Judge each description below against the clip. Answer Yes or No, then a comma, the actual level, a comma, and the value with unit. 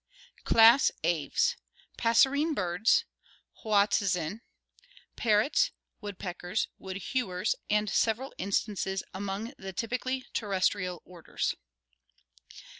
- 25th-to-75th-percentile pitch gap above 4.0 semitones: No, average, 3.7 semitones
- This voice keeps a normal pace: No, slow, 80 wpm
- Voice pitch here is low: No, high, 205 Hz